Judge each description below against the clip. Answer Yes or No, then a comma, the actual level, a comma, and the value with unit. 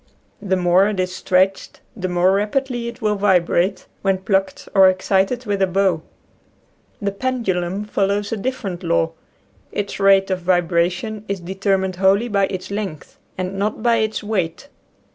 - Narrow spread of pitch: Yes, narrow, 2.1 semitones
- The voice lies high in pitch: Yes, high, 195 Hz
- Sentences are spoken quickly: No, average, 160 wpm